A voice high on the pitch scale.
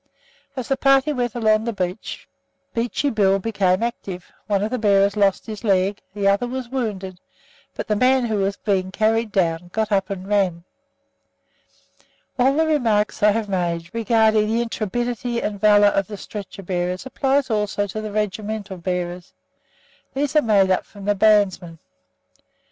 Yes: high, 210 Hz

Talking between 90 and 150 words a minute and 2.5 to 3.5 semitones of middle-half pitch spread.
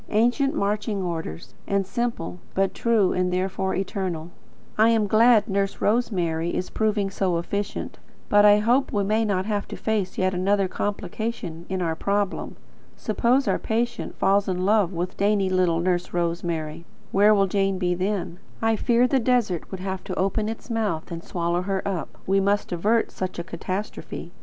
No: average, 170 wpm; average, 2.9 semitones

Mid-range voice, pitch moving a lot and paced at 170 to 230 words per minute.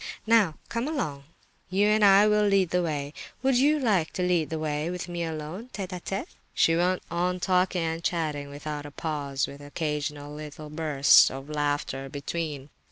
No: medium, 165 Hz; average, 4.1 semitones; average, 180 wpm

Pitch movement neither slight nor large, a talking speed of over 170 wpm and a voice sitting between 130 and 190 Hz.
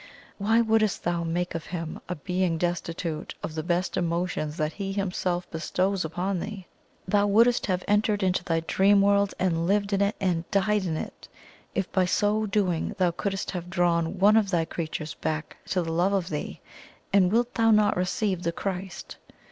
Yes: average, 3.0 semitones; average, 185 wpm; medium, 185 Hz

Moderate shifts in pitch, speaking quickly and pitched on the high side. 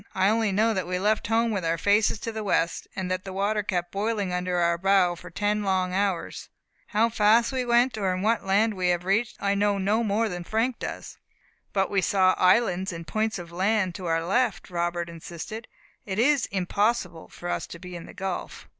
Yes: average, 3.3 semitones; fast, 210 wpm; high, 195 Hz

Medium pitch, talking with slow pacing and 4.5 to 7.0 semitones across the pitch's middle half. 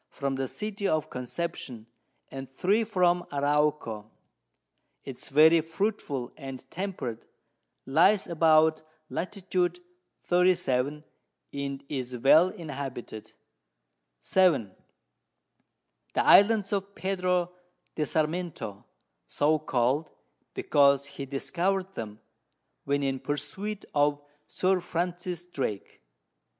Yes: medium, 155 Hz; slow, 95 wpm; average, 5.1 semitones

